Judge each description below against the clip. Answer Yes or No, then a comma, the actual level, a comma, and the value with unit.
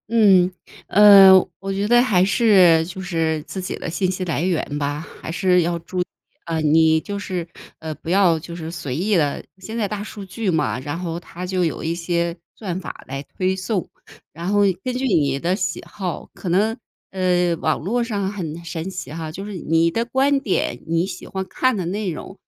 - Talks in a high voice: No, medium, 180 Hz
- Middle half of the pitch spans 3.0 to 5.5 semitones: Yes, average, 3.3 semitones